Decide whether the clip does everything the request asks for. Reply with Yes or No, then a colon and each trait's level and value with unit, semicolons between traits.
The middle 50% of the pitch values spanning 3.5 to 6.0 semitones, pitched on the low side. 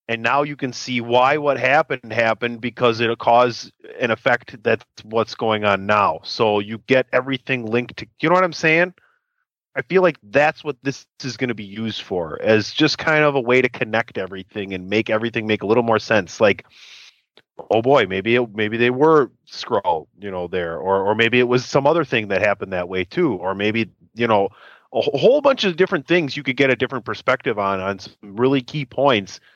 Yes: average, 4.5 semitones; low, 120 Hz